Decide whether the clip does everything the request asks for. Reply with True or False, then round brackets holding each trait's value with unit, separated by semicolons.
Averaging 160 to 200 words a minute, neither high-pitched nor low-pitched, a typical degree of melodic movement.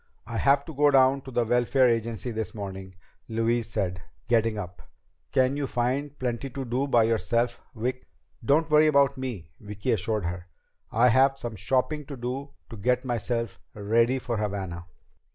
False (170 wpm; 120 Hz; 3.4 semitones)